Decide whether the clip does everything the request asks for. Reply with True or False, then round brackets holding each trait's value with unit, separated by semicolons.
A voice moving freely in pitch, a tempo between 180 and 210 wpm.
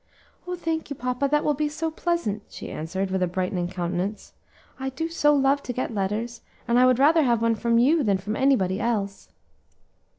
True (6.6 semitones; 200 wpm)